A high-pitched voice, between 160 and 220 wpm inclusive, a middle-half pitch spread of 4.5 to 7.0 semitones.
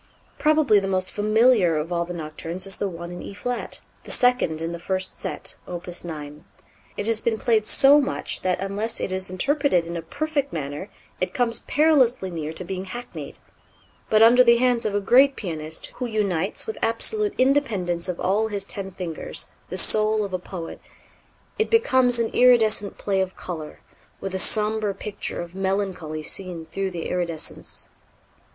Yes: high, 195 Hz; average, 175 wpm; average, 5.1 semitones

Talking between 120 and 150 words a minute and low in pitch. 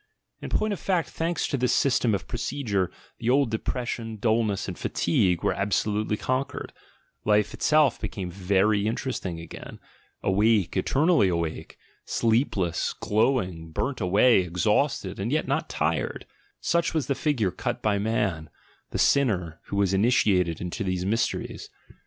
Yes: average, 145 wpm; low, 105 Hz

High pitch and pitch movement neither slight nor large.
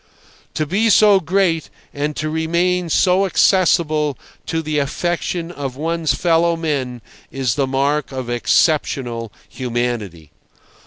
No: medium, 155 Hz; average, 4.5 semitones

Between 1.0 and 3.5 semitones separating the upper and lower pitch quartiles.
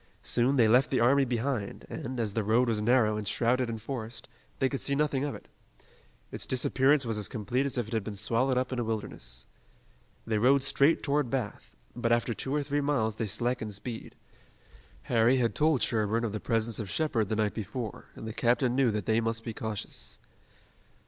Yes: average, 3.0 semitones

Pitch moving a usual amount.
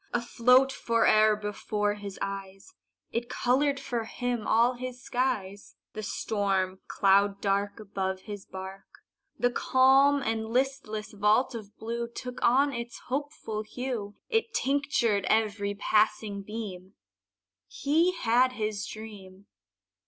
Yes: average, 3.7 semitones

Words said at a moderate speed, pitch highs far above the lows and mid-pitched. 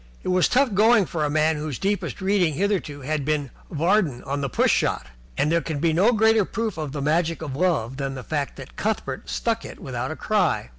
No: fast, 225 wpm; wide, 5.8 semitones; medium, 160 Hz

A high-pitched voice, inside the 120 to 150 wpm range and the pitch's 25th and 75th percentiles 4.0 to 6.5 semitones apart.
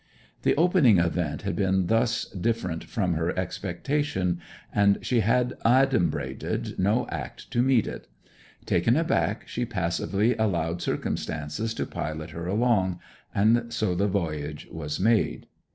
No: low, 100 Hz; slow, 135 wpm; average, 5.3 semitones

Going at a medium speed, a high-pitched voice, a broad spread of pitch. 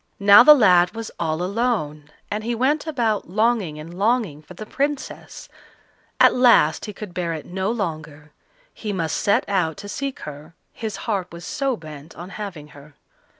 Yes: average, 175 wpm; high, 195 Hz; wide, 6.1 semitones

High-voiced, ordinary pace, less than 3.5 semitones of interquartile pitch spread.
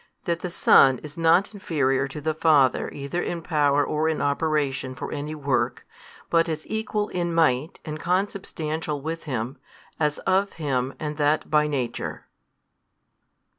No: medium, 150 Hz; average, 150 wpm; average, 2.8 semitones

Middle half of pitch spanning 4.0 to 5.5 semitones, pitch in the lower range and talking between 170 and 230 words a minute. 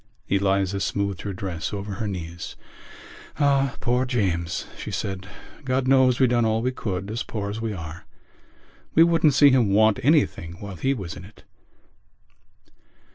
No: average, 5.0 semitones; low, 105 Hz; average, 155 wpm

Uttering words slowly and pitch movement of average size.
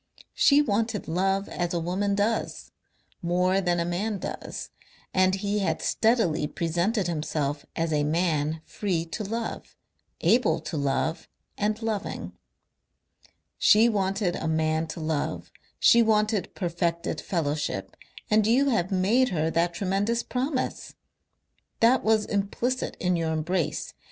Yes: slow, 130 wpm; average, 4.6 semitones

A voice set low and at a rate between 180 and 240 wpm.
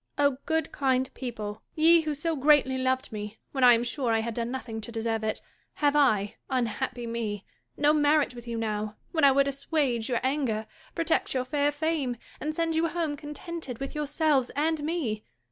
No: very high, 265 Hz; average, 195 wpm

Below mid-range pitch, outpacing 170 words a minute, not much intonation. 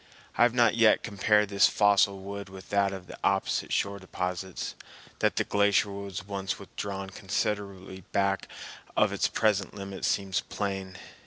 No: low, 100 Hz; average, 155 wpm; narrow, 1.1 semitones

